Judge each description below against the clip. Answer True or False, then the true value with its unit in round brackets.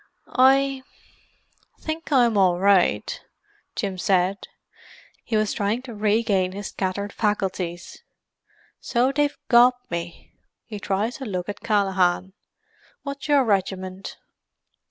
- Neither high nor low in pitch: False (205 Hz)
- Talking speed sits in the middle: False (115 wpm)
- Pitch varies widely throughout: False (4.7 semitones)